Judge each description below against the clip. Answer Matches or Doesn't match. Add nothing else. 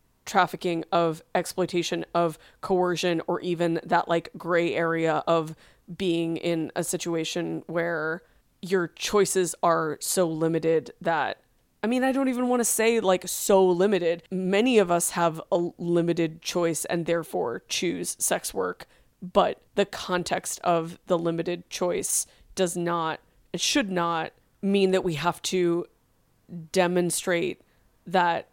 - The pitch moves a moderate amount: Doesn't match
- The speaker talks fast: Doesn't match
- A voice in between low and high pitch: Matches